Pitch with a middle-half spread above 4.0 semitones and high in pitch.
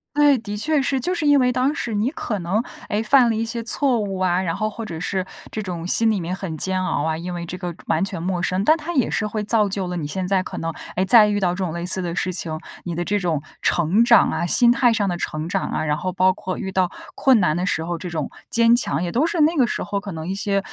Yes: average, 4.7 semitones; high, 195 Hz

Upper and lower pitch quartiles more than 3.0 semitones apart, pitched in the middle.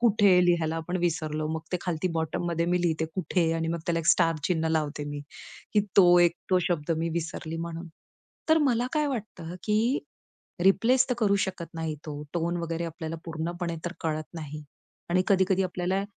No: narrow, 2.6 semitones; medium, 170 Hz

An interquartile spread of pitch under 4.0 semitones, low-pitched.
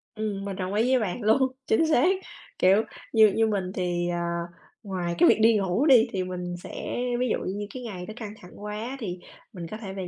No: average, 3.5 semitones; high, 205 Hz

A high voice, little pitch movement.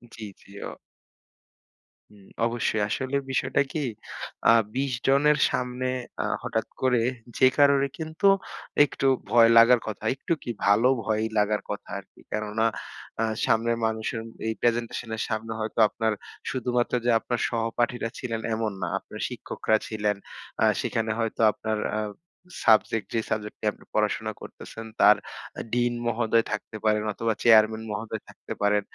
No: low, 115 Hz; narrow, 2.0 semitones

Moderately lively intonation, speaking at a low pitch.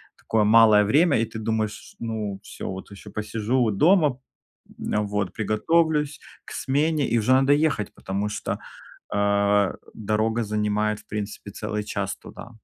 Yes: average, 3.5 semitones; low, 110 Hz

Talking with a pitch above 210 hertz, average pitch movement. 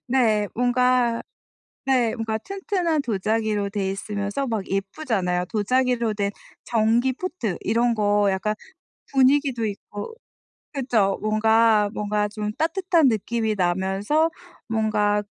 Yes: high, 220 Hz; average, 3.5 semitones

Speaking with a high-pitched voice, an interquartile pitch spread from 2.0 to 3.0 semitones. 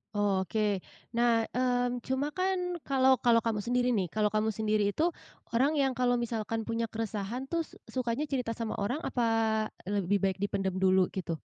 No: high, 230 Hz; average, 3.7 semitones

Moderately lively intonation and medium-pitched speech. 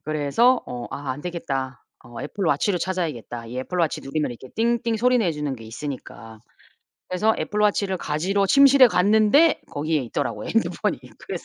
No: wide, 7.5 semitones; medium, 170 Hz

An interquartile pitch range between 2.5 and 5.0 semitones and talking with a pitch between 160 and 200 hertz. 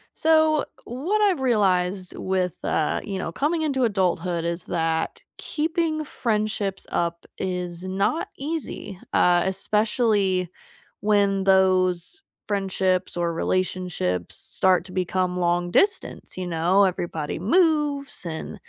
No: wide, 5.5 semitones; high, 190 Hz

